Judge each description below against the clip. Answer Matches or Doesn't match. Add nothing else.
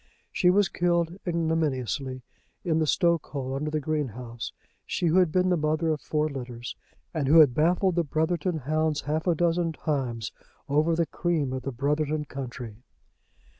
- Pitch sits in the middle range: Matches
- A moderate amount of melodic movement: Matches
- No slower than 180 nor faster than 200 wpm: Doesn't match